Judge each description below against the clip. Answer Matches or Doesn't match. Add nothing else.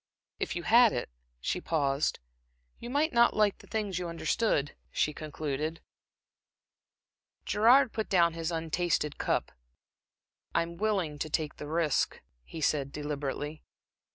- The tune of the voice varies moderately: Doesn't match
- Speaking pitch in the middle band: Matches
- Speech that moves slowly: Matches